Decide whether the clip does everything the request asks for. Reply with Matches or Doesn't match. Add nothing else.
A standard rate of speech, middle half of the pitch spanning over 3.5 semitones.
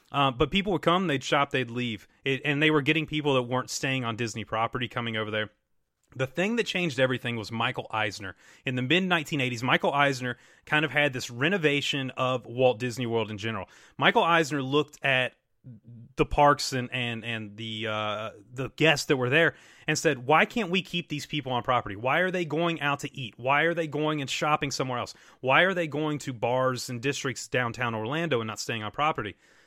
Doesn't match